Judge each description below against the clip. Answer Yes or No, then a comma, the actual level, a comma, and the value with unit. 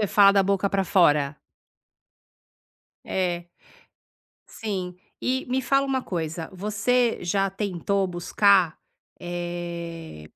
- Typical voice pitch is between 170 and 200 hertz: Yes, high, 190 Hz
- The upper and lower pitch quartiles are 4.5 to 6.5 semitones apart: No, average, 2.9 semitones